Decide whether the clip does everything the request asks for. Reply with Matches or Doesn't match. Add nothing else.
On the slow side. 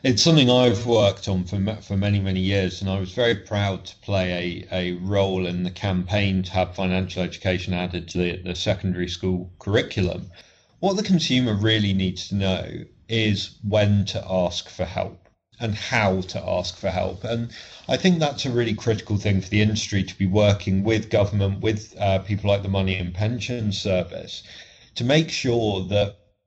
Doesn't match